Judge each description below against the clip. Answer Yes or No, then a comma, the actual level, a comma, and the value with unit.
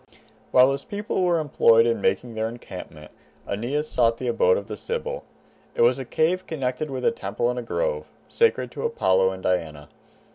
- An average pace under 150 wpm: No, average, 180 wpm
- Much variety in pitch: Yes, wide, 8.2 semitones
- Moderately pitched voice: No, low, 125 Hz